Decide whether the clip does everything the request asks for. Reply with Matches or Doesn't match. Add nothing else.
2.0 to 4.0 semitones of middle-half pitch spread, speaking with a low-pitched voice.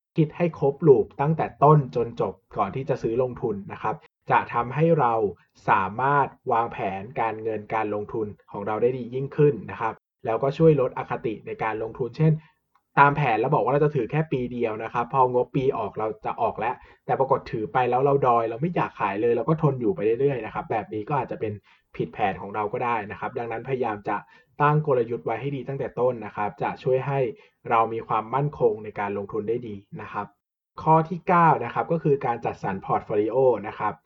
Doesn't match